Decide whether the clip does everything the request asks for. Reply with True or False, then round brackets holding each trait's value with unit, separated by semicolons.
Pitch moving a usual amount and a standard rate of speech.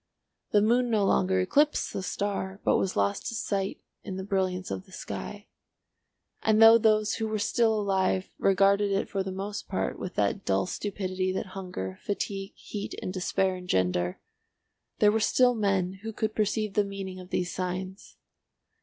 False (2.1 semitones; 170 wpm)